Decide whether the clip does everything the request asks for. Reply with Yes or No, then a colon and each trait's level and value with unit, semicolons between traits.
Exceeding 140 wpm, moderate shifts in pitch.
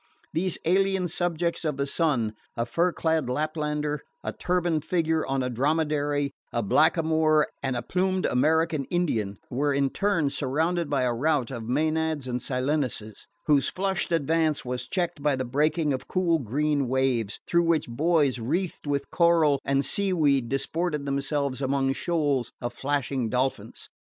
Yes: average, 150 wpm; average, 3.7 semitones